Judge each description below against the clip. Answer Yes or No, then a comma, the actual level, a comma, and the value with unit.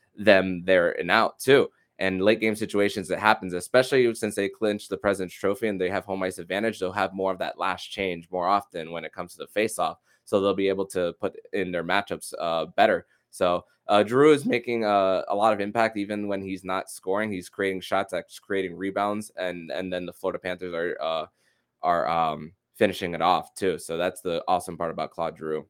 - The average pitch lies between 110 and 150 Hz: No, low, 100 Hz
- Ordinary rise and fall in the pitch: No, narrow, 2.2 semitones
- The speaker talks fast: Yes, fast, 215 wpm